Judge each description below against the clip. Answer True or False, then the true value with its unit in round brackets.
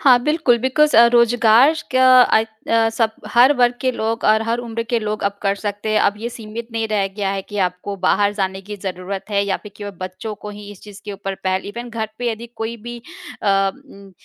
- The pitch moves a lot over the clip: False (2.9 semitones)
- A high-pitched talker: True (215 Hz)